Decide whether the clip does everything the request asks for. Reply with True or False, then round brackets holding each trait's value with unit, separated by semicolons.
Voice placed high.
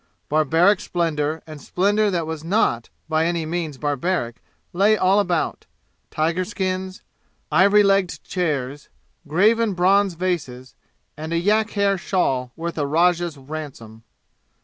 False (170 Hz)